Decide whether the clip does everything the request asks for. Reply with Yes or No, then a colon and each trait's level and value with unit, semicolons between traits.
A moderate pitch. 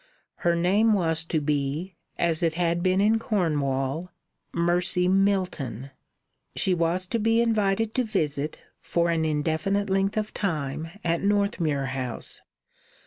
Yes: medium, 175 Hz